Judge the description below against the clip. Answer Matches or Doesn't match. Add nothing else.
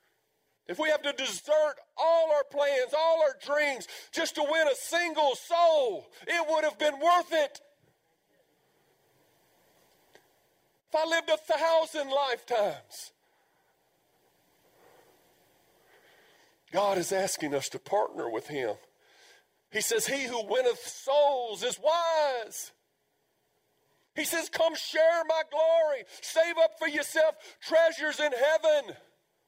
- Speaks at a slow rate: Matches